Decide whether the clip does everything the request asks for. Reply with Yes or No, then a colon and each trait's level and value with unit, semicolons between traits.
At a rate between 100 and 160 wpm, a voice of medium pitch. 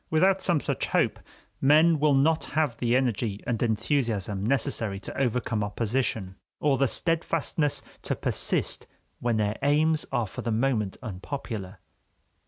No: average, 140 wpm; low, 125 Hz